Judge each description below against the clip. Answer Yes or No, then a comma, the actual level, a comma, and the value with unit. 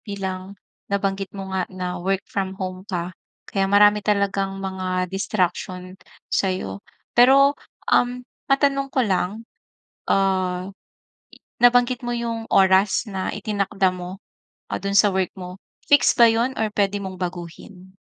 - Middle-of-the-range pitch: No, high, 195 Hz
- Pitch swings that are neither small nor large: No, narrow, 2.3 semitones